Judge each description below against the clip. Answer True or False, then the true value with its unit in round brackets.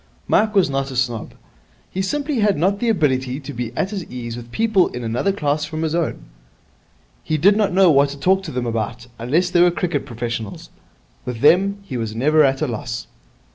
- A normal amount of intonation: False (7.5 semitones)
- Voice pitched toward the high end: False (150 Hz)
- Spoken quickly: True (210 wpm)